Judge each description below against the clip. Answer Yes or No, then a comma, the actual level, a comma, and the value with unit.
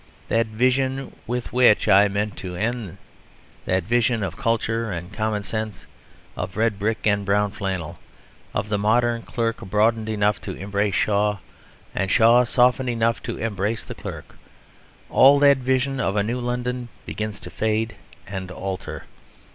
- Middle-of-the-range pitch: No, low, 110 Hz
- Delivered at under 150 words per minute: No, average, 155 wpm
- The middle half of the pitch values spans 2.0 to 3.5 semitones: Yes, average, 3.0 semitones